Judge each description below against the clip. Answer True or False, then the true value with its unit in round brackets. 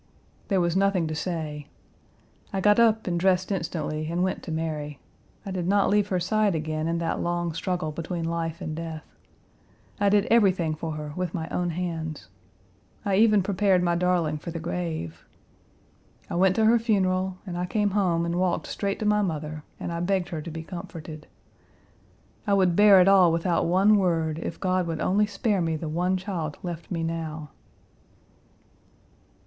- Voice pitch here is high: False (175 Hz)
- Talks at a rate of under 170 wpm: False (180 wpm)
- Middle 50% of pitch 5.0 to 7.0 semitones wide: False (2.9 semitones)